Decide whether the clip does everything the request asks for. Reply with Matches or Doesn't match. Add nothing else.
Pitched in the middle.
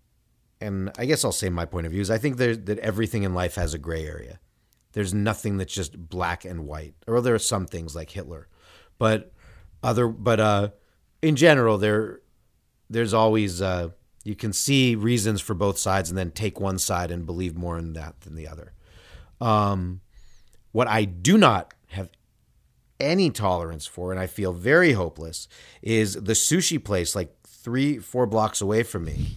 Doesn't match